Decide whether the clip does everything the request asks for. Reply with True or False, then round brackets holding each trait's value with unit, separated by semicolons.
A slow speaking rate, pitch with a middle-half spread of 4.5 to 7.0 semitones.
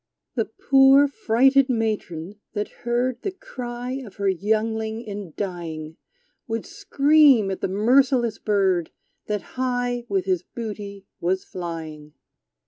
True (125 wpm; 4.8 semitones)